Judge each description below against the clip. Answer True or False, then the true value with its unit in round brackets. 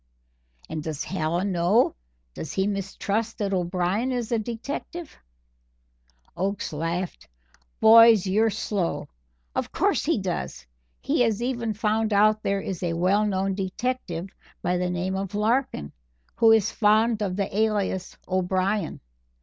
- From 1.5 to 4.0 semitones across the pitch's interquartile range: True (3.4 semitones)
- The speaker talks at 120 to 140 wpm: True (135 wpm)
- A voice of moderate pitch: False (200 Hz)